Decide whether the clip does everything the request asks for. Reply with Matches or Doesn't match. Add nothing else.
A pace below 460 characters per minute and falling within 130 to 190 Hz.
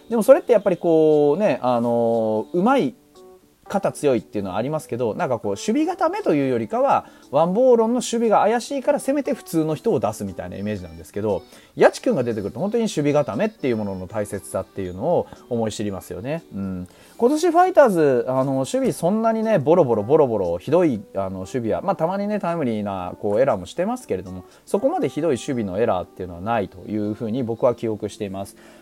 Doesn't match